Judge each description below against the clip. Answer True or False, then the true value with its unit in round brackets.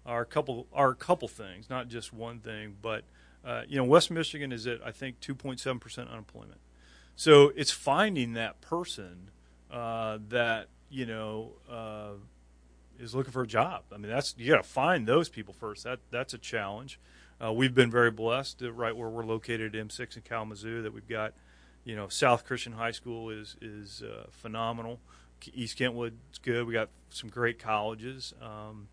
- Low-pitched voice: True (115 Hz)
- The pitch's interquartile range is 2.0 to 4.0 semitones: True (2.6 semitones)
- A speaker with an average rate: True (185 wpm)